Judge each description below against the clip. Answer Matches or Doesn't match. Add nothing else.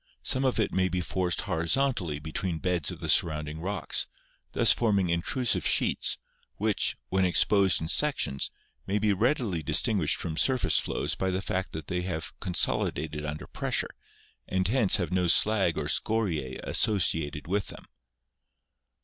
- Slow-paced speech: Doesn't match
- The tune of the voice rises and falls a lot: Doesn't match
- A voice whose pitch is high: Doesn't match